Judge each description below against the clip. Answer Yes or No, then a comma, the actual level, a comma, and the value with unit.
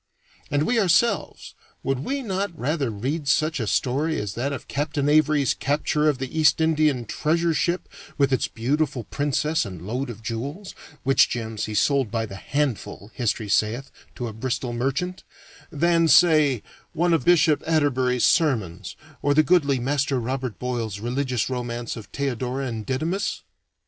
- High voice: No, medium, 140 Hz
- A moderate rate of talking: Yes, average, 160 wpm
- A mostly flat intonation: No, average, 4.3 semitones